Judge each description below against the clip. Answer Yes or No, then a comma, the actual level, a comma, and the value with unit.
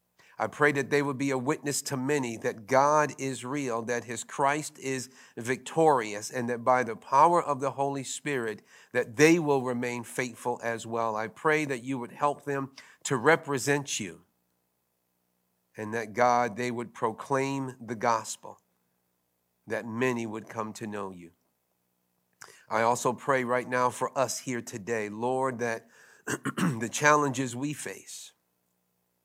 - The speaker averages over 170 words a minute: No, average, 155 wpm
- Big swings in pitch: No, average, 4.5 semitones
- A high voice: No, low, 120 Hz